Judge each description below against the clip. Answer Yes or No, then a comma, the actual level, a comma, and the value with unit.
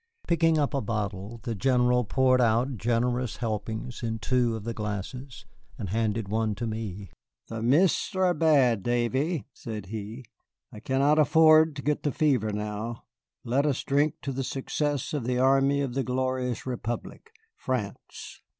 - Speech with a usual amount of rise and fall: Yes, average, 3.7 semitones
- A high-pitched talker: No, low, 125 Hz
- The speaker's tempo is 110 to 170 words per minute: Yes, average, 155 wpm